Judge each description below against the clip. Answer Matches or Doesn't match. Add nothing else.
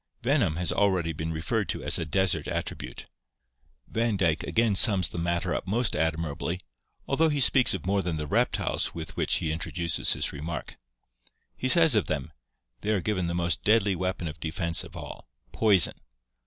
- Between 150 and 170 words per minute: Doesn't match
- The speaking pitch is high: Doesn't match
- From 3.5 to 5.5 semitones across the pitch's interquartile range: Matches